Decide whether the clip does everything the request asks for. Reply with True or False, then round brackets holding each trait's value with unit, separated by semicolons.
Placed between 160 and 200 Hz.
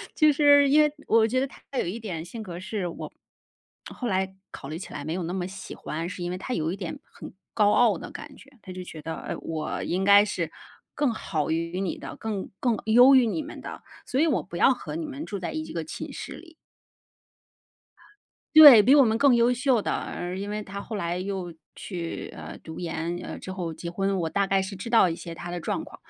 True (195 Hz)